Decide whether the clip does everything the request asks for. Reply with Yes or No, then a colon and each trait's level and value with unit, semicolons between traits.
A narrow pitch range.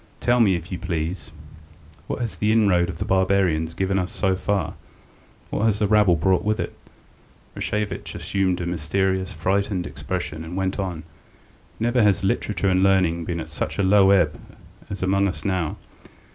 Yes: narrow, 2.3 semitones